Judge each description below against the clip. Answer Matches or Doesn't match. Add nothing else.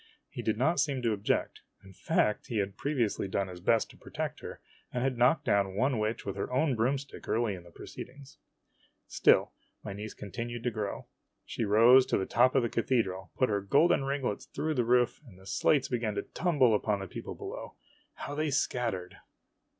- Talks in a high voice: Doesn't match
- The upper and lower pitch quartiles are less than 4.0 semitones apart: Doesn't match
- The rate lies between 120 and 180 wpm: Doesn't match